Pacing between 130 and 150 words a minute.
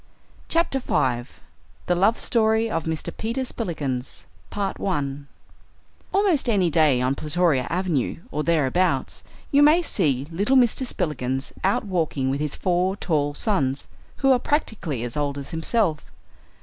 Yes: slow, 135 wpm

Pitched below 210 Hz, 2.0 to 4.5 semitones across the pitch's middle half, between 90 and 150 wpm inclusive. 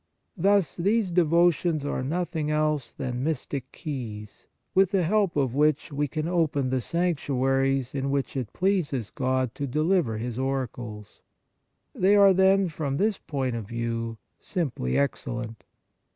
No: medium, 140 Hz; average, 5.2 semitones; average, 140 wpm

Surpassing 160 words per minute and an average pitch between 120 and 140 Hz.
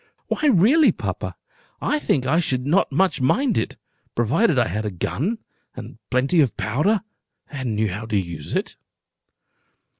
No: average, 155 wpm; low, 135 Hz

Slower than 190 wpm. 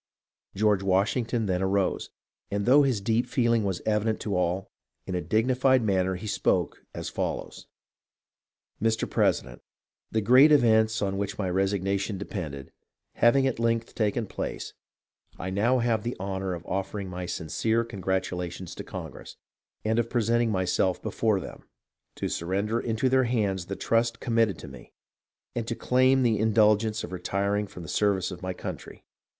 Yes: average, 165 wpm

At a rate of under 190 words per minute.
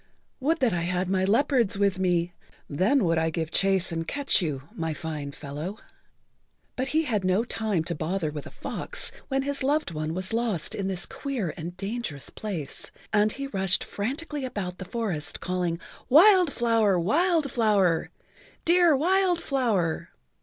Yes: average, 165 wpm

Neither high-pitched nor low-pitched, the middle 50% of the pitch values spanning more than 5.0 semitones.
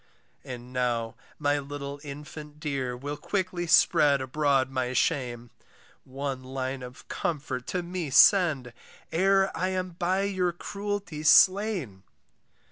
Yes: medium, 145 Hz; wide, 5.6 semitones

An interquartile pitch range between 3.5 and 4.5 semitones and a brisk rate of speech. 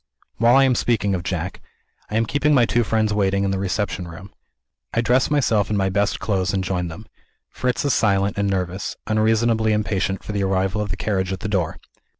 No: average, 2.7 semitones; fast, 210 wpm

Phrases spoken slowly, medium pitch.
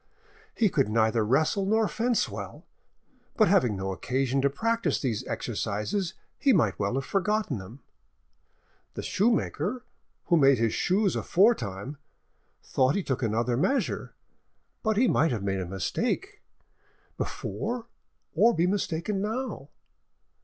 Yes: slow, 130 wpm; medium, 160 Hz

